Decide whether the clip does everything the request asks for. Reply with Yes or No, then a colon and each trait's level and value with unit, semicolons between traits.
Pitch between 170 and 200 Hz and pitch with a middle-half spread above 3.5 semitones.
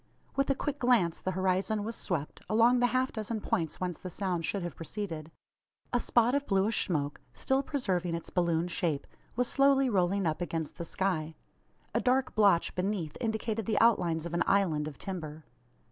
Yes: high, 190 Hz; average, 5.3 semitones